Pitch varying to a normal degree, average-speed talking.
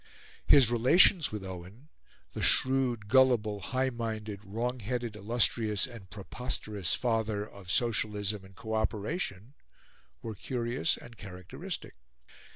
No: average, 3.2 semitones; slow, 115 wpm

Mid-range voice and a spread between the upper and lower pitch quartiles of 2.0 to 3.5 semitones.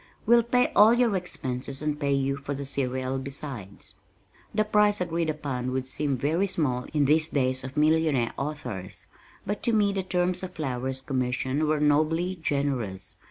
No: medium, 145 Hz; average, 5.2 semitones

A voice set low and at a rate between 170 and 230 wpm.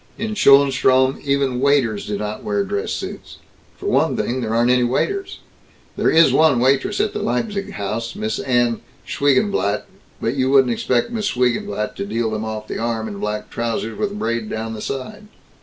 Yes: low, 125 Hz; average, 180 wpm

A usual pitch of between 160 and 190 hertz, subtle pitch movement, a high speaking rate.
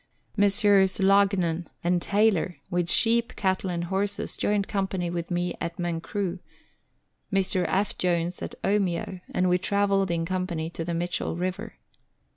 No: medium, 185 Hz; narrow, 2.3 semitones; average, 140 wpm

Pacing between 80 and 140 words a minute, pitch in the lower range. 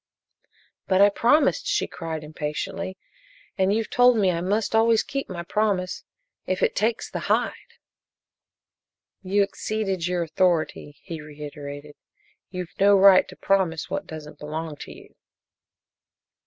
No: slow, 135 wpm; medium, 185 Hz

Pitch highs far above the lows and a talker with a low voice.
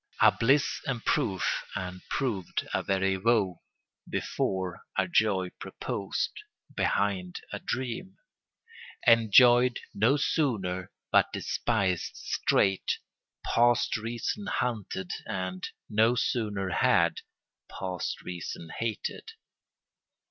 No: average, 4.4 semitones; low, 105 Hz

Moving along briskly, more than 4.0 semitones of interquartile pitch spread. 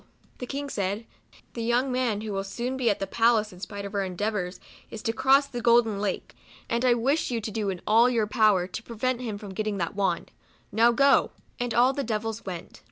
No: fast, 240 wpm; average, 3.2 semitones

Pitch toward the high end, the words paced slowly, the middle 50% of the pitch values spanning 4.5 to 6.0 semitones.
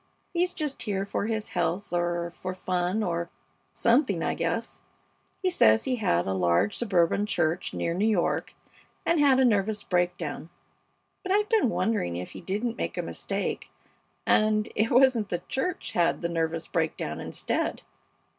No: high, 200 Hz; average, 160 wpm; wide, 5.5 semitones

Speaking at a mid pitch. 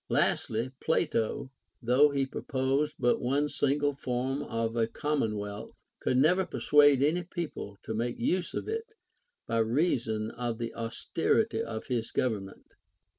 No: low, 130 Hz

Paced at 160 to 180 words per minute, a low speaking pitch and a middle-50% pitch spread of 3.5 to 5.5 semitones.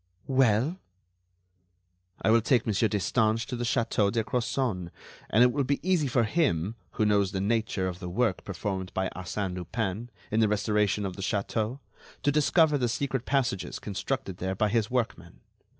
Yes: average, 170 wpm; low, 110 Hz; average, 4.0 semitones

